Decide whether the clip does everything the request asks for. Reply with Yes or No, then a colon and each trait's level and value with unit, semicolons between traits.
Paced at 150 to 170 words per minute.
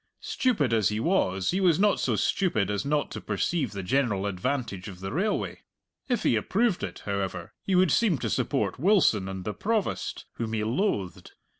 No: average, 185 wpm